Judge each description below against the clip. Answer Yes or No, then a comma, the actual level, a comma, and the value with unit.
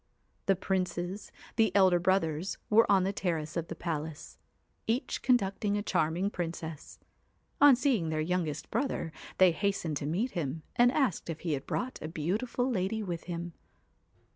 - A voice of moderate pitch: Yes, medium, 180 Hz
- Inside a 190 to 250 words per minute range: No, average, 160 wpm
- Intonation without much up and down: No, average, 4.1 semitones